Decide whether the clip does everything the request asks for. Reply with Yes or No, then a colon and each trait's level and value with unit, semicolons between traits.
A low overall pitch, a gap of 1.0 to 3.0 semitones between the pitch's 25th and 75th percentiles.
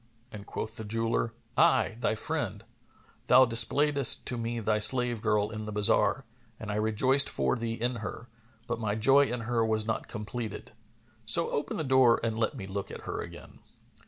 Yes: low, 115 Hz; narrow, 2.4 semitones